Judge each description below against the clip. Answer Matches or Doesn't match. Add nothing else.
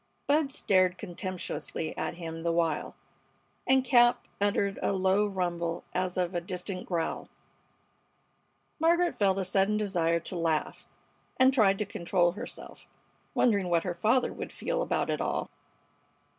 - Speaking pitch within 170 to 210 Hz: Matches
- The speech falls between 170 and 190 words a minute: Doesn't match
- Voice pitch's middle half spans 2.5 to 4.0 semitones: Matches